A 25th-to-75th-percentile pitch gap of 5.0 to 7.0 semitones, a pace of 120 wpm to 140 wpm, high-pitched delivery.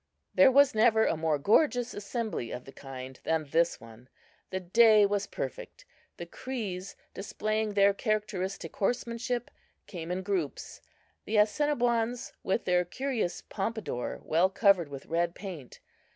Yes: average, 5.3 semitones; slow, 135 wpm; high, 200 Hz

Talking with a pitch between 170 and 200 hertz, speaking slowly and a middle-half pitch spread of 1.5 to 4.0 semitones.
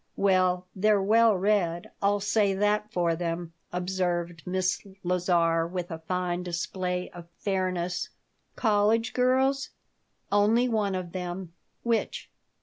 Yes: medium, 185 Hz; slow, 120 wpm; average, 2.9 semitones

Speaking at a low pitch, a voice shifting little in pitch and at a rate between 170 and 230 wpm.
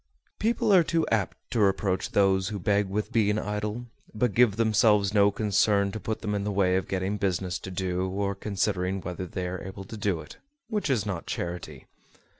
Yes: low, 100 Hz; narrow, 2.1 semitones; average, 200 wpm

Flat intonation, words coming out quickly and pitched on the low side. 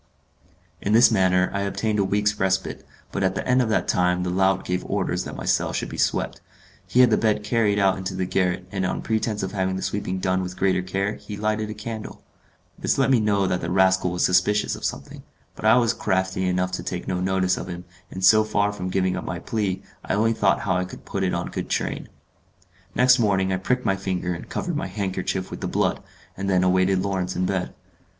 Yes: narrow, 2.2 semitones; fast, 230 wpm; very low, 95 Hz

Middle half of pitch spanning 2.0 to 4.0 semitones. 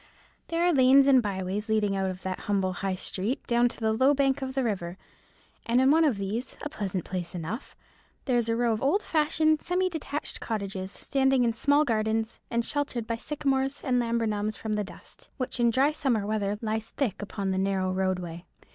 No: average, 5.2 semitones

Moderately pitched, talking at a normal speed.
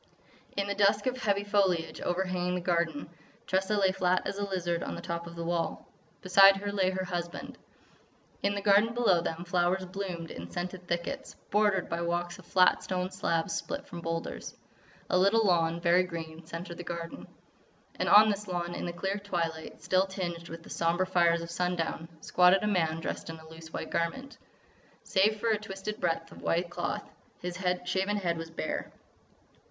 Yes: medium, 180 Hz; average, 185 wpm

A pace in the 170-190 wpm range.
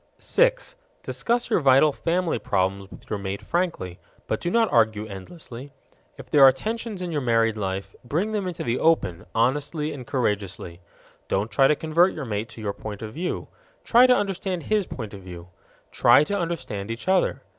Yes: average, 185 wpm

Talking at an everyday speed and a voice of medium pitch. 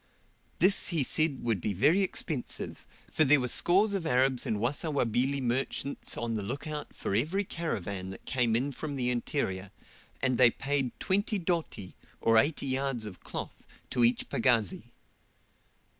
No: average, 160 wpm; low, 130 Hz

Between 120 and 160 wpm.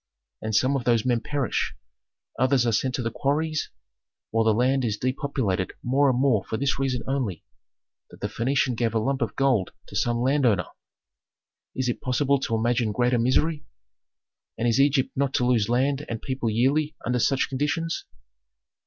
No: average, 175 wpm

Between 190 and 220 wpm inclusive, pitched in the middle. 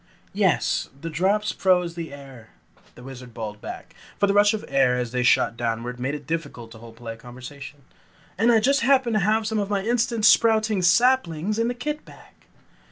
Yes: average, 195 wpm; medium, 175 Hz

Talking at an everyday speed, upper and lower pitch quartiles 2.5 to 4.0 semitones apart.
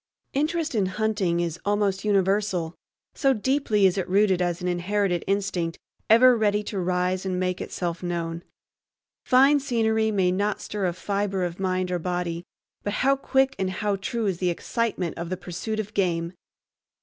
Yes: average, 170 wpm; average, 3.1 semitones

